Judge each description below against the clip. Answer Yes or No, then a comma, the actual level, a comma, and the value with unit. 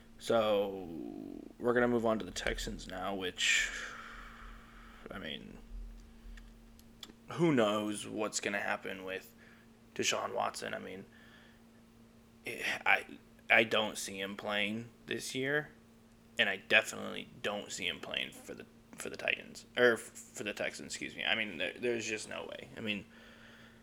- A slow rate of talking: No, average, 145 wpm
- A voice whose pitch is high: No, low, 115 Hz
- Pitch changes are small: Yes, narrow, 1.4 semitones